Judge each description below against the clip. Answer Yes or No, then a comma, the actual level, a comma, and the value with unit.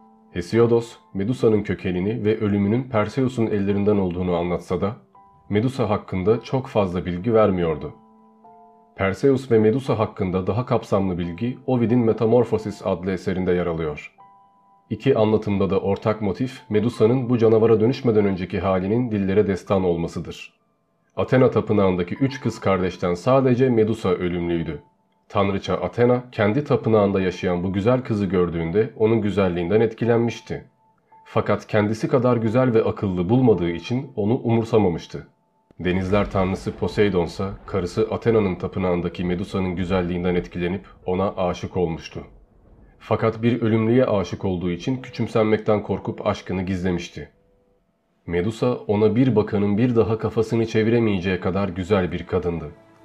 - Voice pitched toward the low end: Yes, low, 105 Hz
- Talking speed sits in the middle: Yes, average, 120 wpm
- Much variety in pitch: No, average, 3.8 semitones